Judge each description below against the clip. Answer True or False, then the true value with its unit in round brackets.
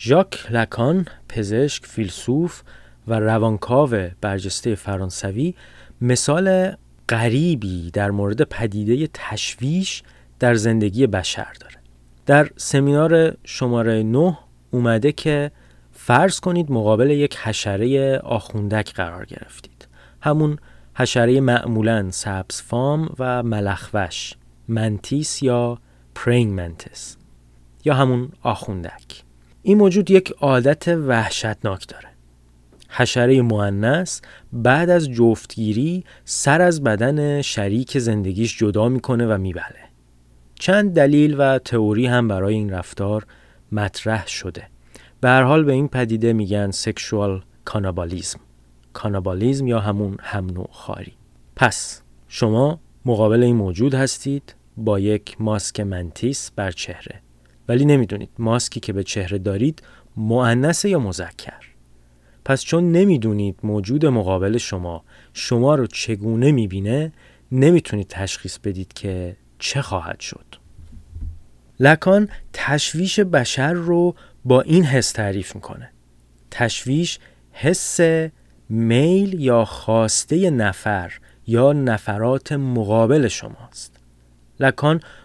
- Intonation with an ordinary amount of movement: False (6.1 semitones)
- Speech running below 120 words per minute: True (105 wpm)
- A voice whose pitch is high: False (115 Hz)